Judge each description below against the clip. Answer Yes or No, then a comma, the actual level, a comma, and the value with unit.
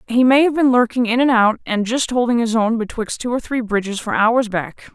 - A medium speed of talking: No, fast, 255 wpm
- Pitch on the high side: Yes, high, 235 Hz